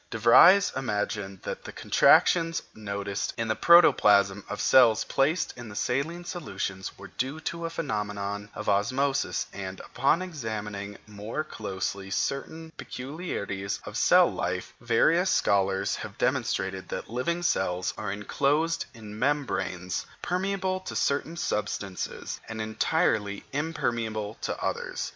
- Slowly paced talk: Yes, slow, 125 wpm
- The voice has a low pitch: Yes, low, 110 Hz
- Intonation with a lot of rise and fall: Yes, wide, 7.4 semitones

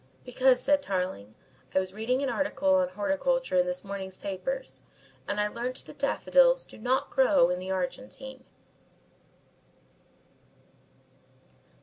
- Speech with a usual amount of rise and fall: No, wide, 6.2 semitones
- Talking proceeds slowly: Yes, slow, 125 wpm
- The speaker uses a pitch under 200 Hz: No, very high, 255 Hz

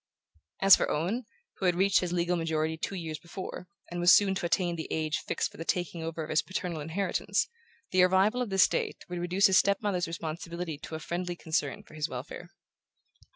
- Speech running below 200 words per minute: No, fast, 205 wpm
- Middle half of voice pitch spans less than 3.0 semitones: Yes, narrow, 2.6 semitones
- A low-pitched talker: No, medium, 175 Hz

